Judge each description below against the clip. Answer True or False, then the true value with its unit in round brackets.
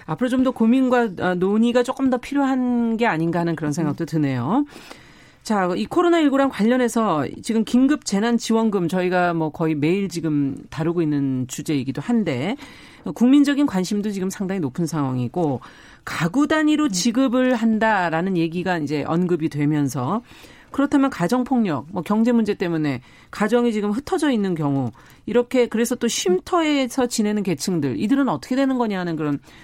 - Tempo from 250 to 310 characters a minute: False (345 characters per minute)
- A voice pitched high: True (210 Hz)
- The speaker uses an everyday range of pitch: False (7.4 semitones)